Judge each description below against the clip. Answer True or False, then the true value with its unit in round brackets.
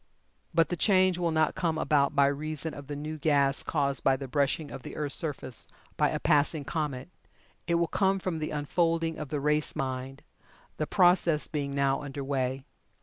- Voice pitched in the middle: True (150 Hz)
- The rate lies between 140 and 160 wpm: False (190 wpm)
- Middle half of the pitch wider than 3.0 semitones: False (2.7 semitones)